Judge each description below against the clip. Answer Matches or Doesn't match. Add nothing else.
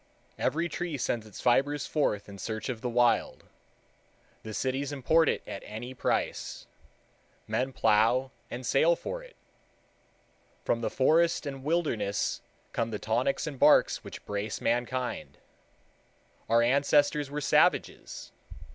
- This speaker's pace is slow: Matches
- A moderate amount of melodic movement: Matches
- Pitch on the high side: Doesn't match